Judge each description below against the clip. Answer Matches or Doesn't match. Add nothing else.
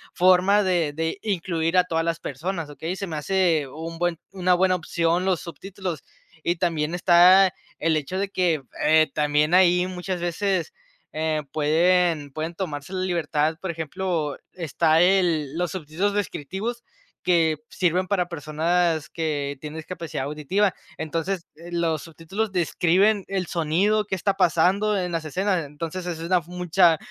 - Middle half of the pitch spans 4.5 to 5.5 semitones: Doesn't match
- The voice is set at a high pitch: Doesn't match